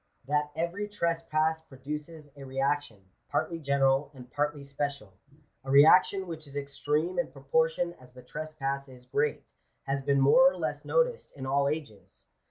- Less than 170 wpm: Yes, average, 160 wpm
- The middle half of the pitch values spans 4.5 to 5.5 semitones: No, average, 2.9 semitones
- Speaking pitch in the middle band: Yes, medium, 145 Hz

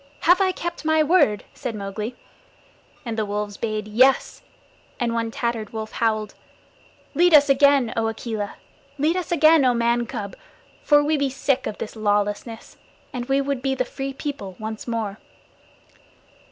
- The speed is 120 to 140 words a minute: No, average, 160 wpm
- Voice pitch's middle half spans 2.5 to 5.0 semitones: Yes, average, 4.6 semitones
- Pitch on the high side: Yes, high, 240 Hz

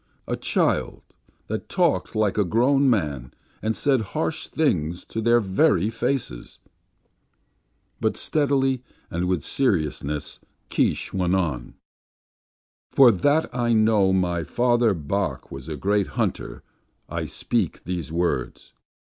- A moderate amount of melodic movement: No, wide, 5.9 semitones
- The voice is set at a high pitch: No, low, 100 Hz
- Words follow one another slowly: Yes, slow, 120 wpm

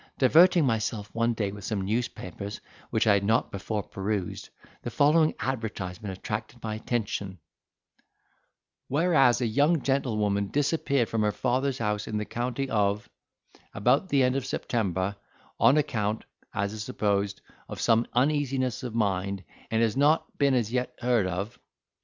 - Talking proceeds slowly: No, average, 150 wpm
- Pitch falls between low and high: No, low, 115 Hz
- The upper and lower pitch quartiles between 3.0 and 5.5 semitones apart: Yes, average, 4.3 semitones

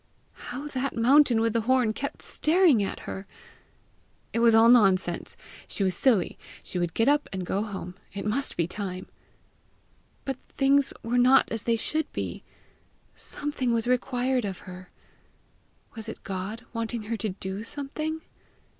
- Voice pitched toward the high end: Yes, high, 230 Hz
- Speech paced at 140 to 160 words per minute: Yes, average, 155 wpm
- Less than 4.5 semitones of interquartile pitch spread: No, average, 4.8 semitones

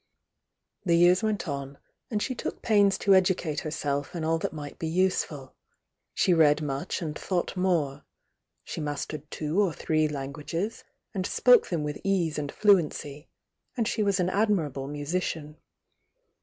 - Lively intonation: No, average, 4.3 semitones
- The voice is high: No, medium, 165 Hz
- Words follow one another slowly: No, average, 155 wpm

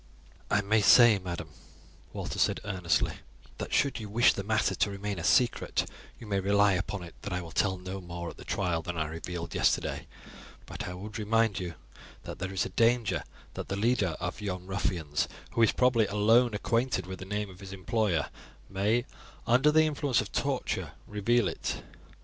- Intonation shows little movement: No, average, 3.7 semitones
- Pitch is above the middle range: No, low, 100 Hz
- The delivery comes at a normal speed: Yes, average, 190 wpm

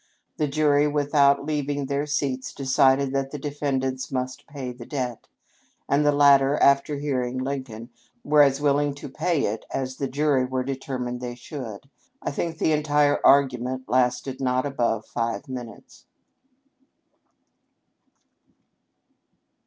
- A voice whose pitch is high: No, low, 135 Hz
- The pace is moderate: No, slow, 130 wpm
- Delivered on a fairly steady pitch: Yes, narrow, 2.1 semitones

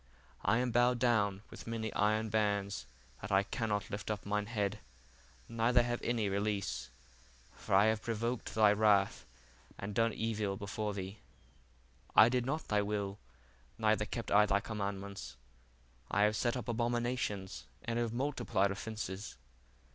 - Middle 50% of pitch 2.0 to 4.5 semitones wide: Yes, narrow, 2.4 semitones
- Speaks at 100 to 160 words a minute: Yes, average, 145 wpm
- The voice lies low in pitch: Yes, low, 105 Hz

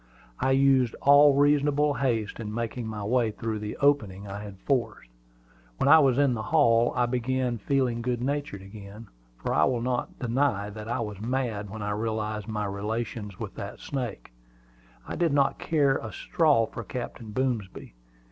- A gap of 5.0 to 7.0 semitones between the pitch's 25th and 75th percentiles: No, average, 4.2 semitones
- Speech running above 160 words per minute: Yes, average, 175 wpm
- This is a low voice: Yes, low, 115 Hz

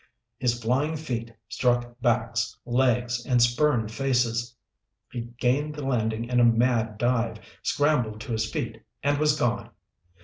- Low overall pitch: Yes, low, 120 Hz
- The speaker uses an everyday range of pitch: No, narrow, 2.1 semitones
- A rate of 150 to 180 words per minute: No, average, 140 wpm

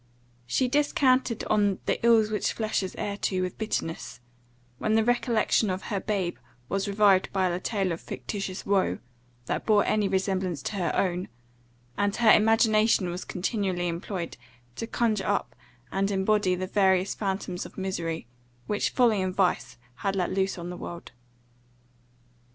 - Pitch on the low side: No, high, 195 Hz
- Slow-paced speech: No, average, 155 wpm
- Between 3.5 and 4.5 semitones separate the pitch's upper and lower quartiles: No, average, 2.7 semitones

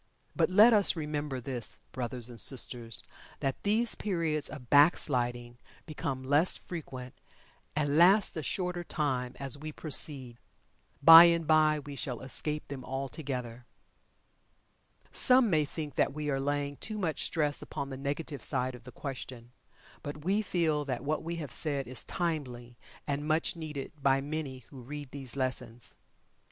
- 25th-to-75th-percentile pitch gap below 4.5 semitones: Yes, average, 3.5 semitones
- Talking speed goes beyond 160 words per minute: No, average, 155 wpm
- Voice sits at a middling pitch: Yes, medium, 145 Hz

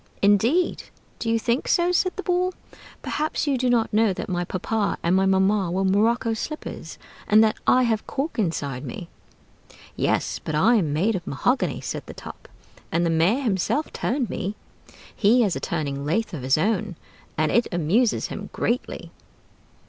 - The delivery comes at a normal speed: Yes, average, 180 wpm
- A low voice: No, high, 215 Hz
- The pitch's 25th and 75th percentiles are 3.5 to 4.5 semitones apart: No, wide, 5.6 semitones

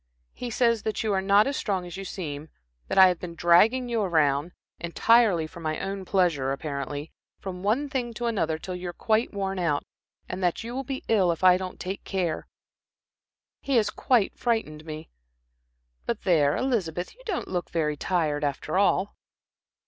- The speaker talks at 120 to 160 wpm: No, average, 185 wpm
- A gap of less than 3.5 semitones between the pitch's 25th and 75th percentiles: No, average, 5.1 semitones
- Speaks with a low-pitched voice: No, medium, 185 Hz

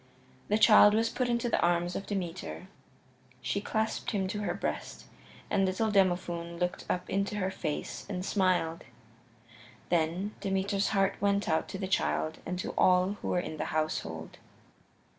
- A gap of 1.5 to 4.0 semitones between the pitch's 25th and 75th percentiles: Yes, average, 2.9 semitones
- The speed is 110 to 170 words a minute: Yes, average, 160 wpm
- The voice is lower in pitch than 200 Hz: Yes, high, 190 Hz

